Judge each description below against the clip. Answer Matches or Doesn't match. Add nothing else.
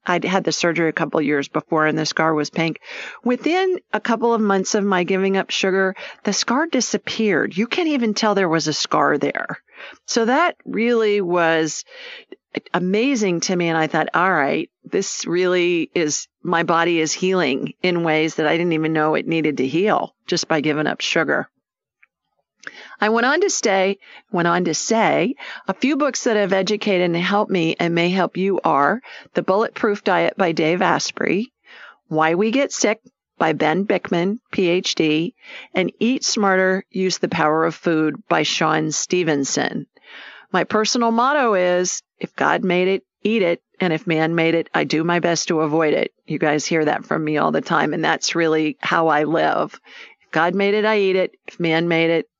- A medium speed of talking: Matches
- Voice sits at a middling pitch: Matches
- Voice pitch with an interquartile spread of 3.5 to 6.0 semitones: Matches